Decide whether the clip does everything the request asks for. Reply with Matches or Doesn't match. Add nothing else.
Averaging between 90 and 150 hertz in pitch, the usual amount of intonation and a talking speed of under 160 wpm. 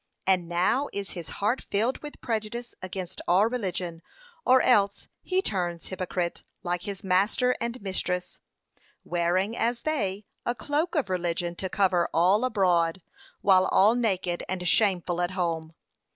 Doesn't match